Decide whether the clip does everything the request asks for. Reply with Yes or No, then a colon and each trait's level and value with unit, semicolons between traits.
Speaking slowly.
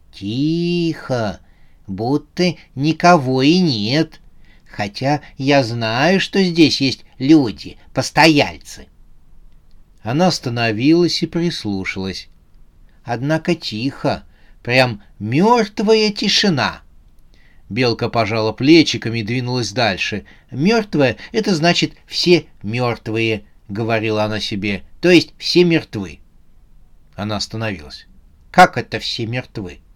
Yes: slow, 90 wpm